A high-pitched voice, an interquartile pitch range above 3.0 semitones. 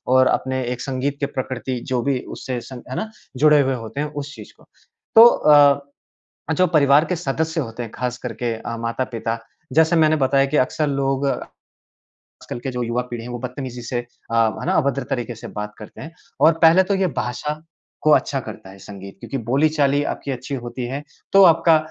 No: low, 135 Hz; average, 3.6 semitones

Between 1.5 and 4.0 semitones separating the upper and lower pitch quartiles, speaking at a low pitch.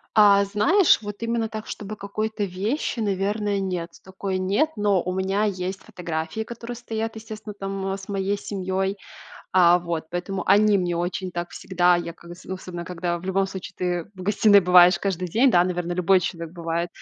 No: average, 2.7 semitones; high, 190 Hz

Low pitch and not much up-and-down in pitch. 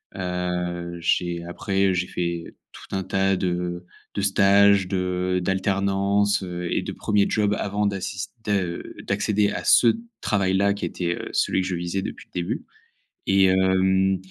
Yes: very low, 95 Hz; narrow, 1.8 semitones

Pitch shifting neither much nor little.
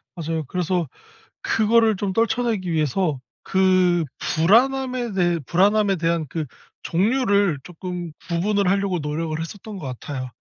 Yes: average, 4.0 semitones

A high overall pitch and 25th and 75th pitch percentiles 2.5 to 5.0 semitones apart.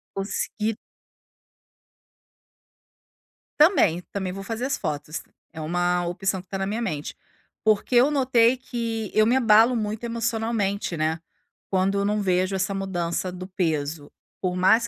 Yes: high, 195 Hz; average, 4.1 semitones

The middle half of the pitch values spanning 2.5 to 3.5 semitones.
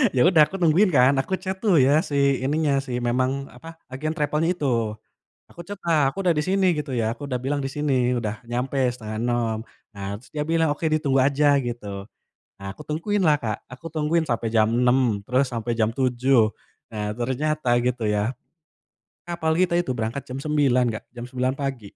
No: average, 4.3 semitones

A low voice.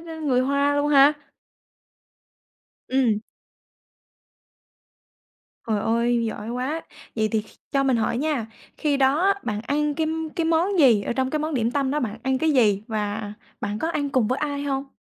No: very high, 265 Hz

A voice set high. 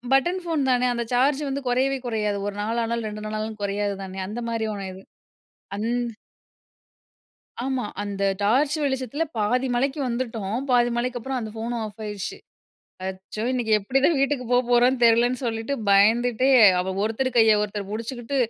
Yes: high, 235 Hz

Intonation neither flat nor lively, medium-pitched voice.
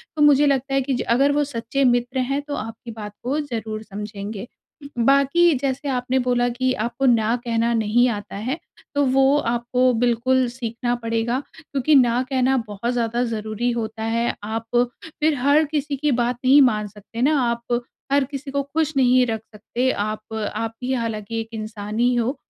No: average, 3.1 semitones; high, 245 Hz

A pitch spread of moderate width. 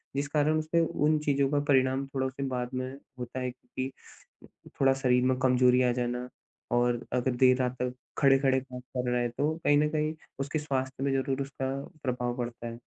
No: narrow, 1.8 semitones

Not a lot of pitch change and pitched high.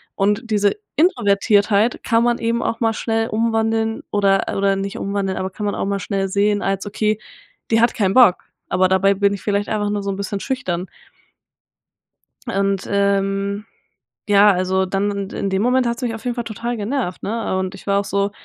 Yes: narrow, 2.3 semitones; high, 205 Hz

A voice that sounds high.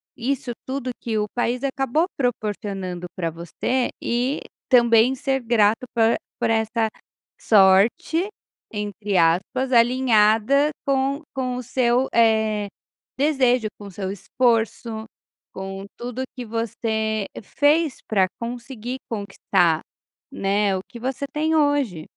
Yes: high, 230 Hz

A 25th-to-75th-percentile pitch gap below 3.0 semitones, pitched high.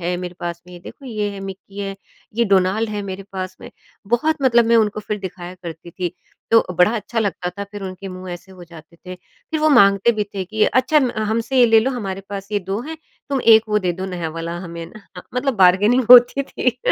No: average, 4.0 semitones; high, 200 Hz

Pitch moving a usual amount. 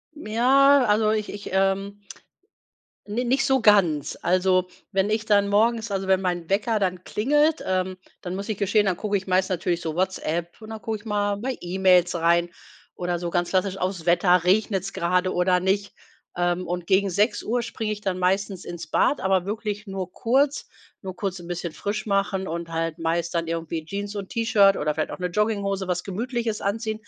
Yes: average, 3.0 semitones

